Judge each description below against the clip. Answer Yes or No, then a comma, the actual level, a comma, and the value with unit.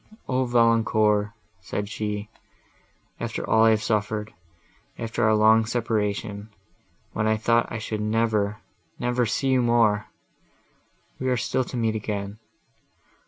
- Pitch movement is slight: Yes, narrow, 1.7 semitones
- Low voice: Yes, low, 110 Hz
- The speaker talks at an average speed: No, slow, 125 wpm